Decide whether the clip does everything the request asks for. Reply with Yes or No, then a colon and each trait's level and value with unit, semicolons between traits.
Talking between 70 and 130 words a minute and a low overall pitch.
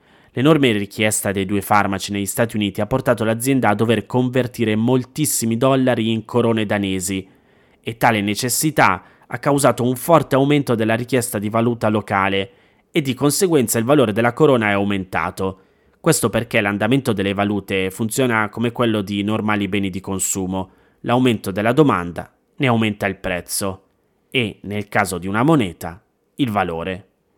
No: average, 150 wpm; low, 110 Hz